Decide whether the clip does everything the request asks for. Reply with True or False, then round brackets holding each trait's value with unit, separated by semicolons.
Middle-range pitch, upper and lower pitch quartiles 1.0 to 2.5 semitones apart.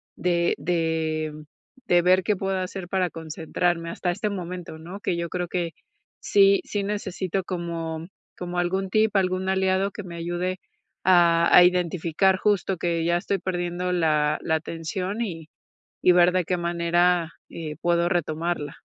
True (175 Hz; 1.9 semitones)